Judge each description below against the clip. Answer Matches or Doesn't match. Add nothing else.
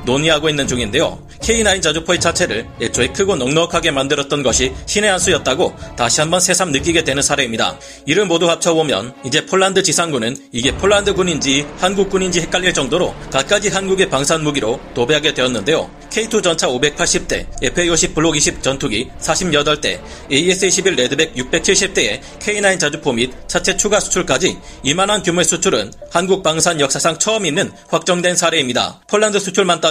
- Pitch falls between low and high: Matches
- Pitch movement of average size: Matches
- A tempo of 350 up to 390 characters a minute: Matches